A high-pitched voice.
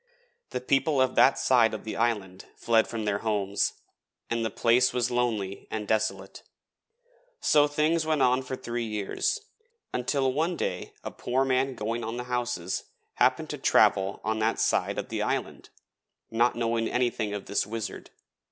No: low, 120 Hz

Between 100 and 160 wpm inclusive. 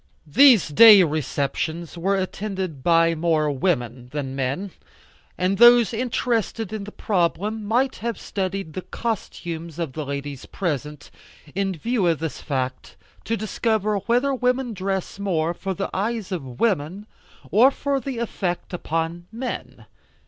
Yes: slow, 135 wpm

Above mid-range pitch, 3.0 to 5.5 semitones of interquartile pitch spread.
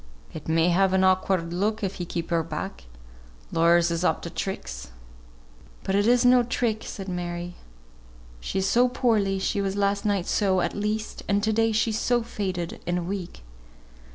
Yes: high, 195 Hz; average, 3.6 semitones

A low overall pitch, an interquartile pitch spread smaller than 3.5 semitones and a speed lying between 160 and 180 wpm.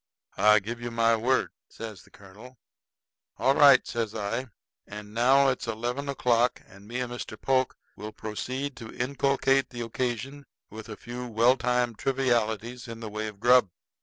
Yes: low, 120 Hz; average, 2.7 semitones; average, 165 wpm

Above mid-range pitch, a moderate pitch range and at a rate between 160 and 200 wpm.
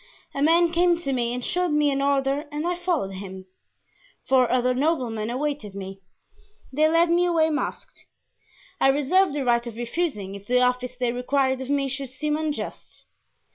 Yes: very high, 275 Hz; average, 4.1 semitones; average, 175 wpm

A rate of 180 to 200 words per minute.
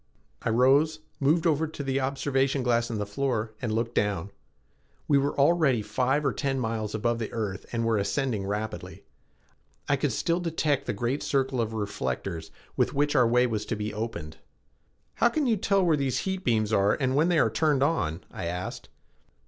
Yes: average, 190 wpm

